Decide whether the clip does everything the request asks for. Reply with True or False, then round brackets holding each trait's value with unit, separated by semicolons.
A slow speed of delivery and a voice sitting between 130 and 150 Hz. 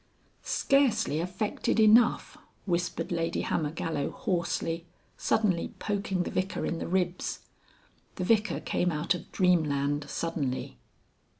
False (110 wpm; 175 Hz)